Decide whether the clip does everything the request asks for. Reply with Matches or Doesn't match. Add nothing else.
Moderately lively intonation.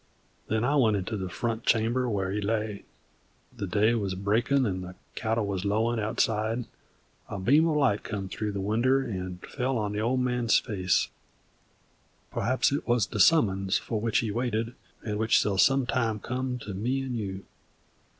Matches